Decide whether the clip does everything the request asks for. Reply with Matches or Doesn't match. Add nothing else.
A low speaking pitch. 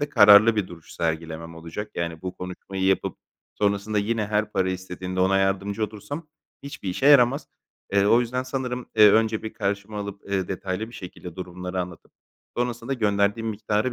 Matches